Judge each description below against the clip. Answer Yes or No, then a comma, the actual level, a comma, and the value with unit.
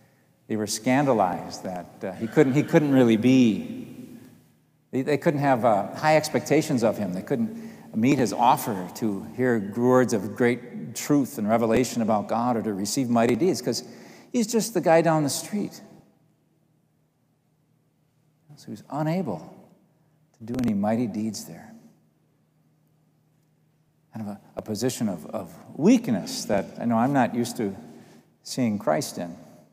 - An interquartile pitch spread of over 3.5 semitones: Yes, average, 4.8 semitones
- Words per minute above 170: No, average, 155 wpm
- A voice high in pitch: No, medium, 140 Hz